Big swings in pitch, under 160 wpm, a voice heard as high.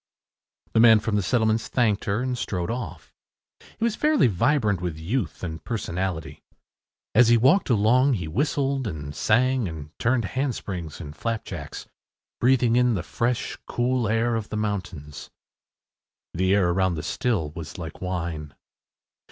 No: wide, 6.1 semitones; average, 150 wpm; low, 105 Hz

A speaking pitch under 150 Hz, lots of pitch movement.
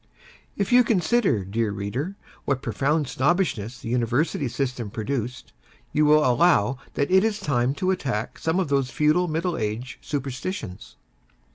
Yes: medium, 140 Hz; wide, 6.0 semitones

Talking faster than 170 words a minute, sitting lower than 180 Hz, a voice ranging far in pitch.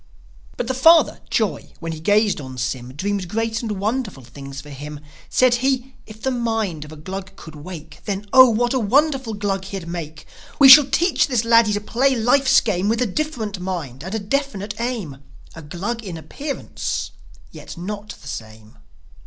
No: average, 185 wpm; high, 205 Hz; wide, 6.8 semitones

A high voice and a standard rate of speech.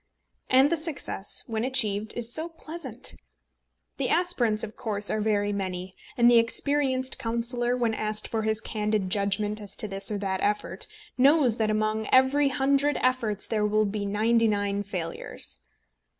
Yes: high, 220 Hz; average, 160 wpm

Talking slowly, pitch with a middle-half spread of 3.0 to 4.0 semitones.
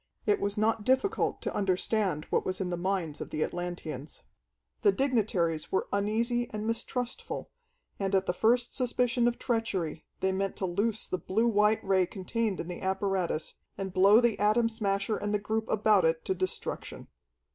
No: average, 175 wpm; average, 3.4 semitones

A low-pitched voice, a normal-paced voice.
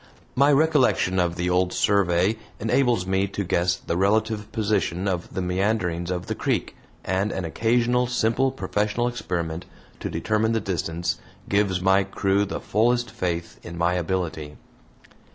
Yes: very low, 95 Hz; average, 150 wpm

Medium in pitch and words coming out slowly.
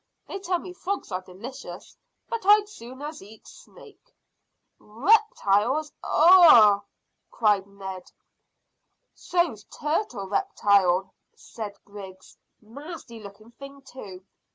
No: high, 230 Hz; slow, 105 wpm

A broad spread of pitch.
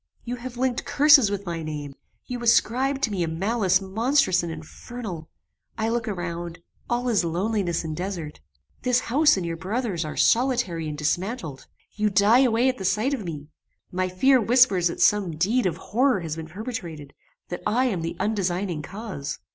Yes: wide, 6.1 semitones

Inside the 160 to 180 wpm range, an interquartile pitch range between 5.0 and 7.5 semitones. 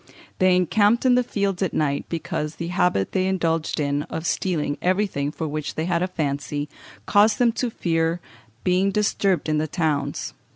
No: average, 175 wpm; average, 4.1 semitones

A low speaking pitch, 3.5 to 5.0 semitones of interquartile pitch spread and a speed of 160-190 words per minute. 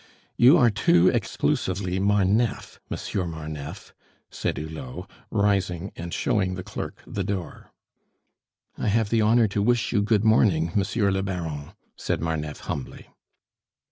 No: very low, 95 Hz; average, 4.0 semitones; slow, 135 wpm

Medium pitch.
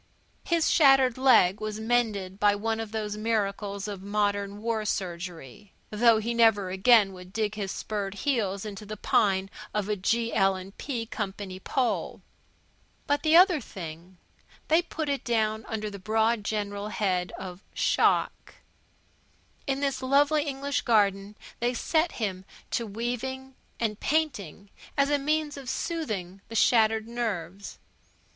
No: high, 215 Hz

